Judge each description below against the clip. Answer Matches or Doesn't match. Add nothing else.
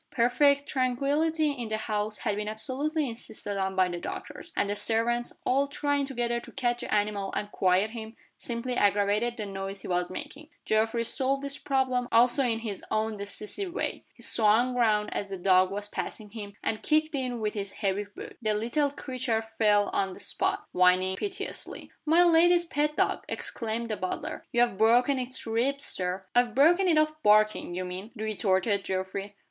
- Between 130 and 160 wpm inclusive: Doesn't match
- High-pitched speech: Matches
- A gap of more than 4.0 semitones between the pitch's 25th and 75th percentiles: Matches